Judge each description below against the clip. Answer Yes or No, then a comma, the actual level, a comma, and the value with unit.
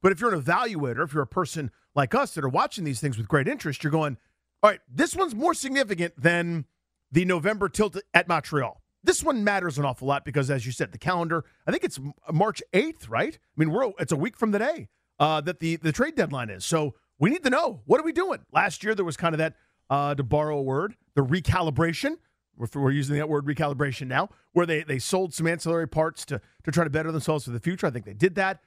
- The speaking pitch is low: No, medium, 160 Hz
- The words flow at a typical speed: No, fast, 245 wpm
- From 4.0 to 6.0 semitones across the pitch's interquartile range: Yes, average, 4.5 semitones